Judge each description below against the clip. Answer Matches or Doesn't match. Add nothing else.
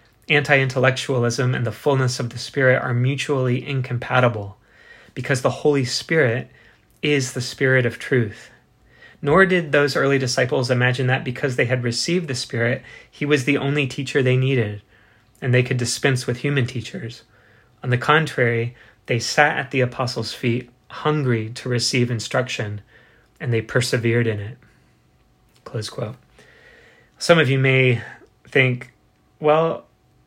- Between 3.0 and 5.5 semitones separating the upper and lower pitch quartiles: Doesn't match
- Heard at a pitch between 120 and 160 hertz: Matches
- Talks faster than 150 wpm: Doesn't match